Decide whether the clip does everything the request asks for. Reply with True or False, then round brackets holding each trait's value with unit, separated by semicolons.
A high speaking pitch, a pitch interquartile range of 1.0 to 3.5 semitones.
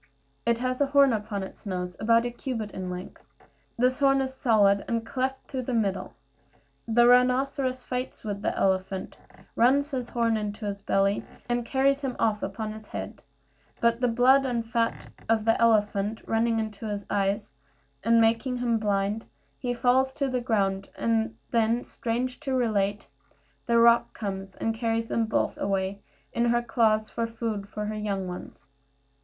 True (230 Hz; 3.1 semitones)